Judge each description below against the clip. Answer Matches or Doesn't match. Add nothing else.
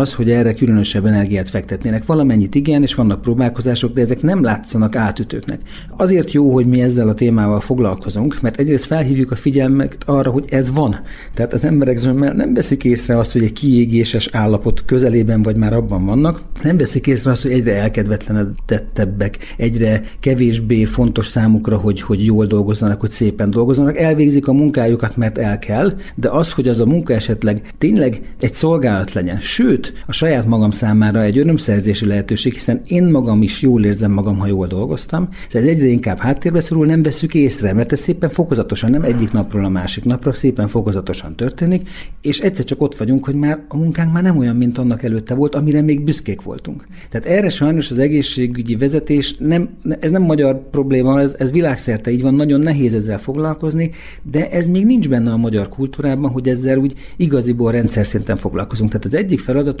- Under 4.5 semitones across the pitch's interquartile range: Doesn't match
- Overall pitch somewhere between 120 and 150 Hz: Matches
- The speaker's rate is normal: Doesn't match